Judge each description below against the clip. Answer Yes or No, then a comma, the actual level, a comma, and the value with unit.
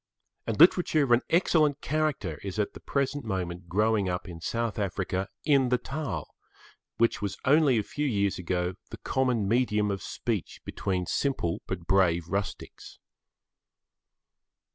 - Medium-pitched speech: No, low, 105 Hz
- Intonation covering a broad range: Yes, wide, 6.4 semitones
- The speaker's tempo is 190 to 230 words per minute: No, average, 145 wpm